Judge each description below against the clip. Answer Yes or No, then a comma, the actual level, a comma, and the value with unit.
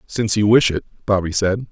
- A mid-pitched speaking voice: No, low, 100 Hz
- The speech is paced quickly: Yes, fast, 210 wpm